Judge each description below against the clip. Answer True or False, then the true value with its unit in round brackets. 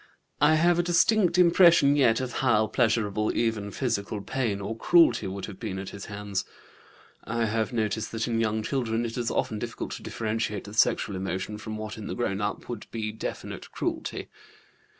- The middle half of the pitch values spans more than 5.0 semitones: False (2.7 semitones)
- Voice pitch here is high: False (110 Hz)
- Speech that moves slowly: False (185 wpm)